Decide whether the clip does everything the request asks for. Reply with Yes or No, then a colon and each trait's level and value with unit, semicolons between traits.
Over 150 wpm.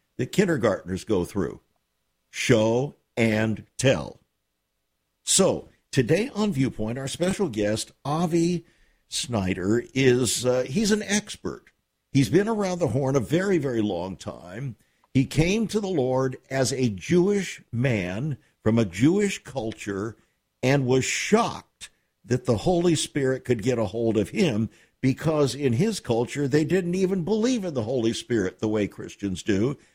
No: average, 145 wpm